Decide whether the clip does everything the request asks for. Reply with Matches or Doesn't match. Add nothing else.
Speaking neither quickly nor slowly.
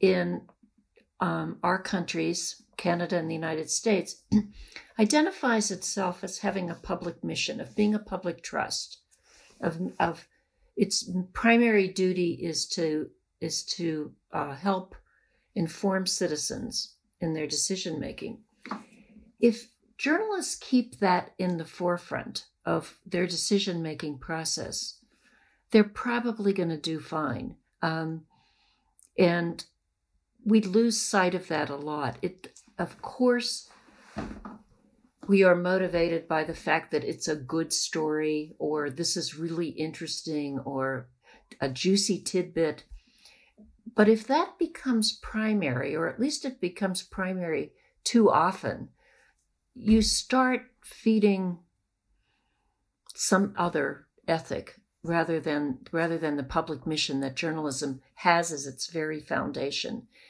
Doesn't match